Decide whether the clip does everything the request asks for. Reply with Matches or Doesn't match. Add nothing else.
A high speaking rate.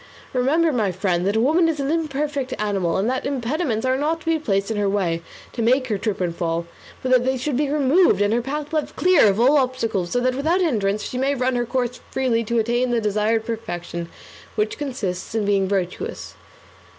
Matches